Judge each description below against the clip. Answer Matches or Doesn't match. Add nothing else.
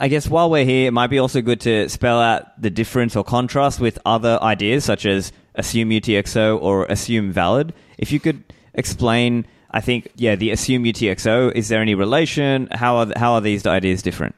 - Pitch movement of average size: Matches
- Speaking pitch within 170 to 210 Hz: Doesn't match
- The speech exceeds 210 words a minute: Doesn't match